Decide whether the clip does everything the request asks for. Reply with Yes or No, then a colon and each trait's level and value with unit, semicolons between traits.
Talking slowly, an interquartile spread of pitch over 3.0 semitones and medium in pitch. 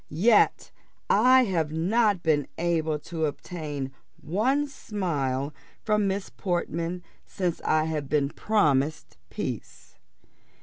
Yes: slow, 105 wpm; average, 5.2 semitones; medium, 165 Hz